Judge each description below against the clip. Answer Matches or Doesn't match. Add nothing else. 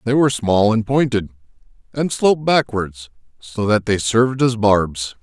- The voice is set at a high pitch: Doesn't match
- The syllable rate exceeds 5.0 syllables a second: Doesn't match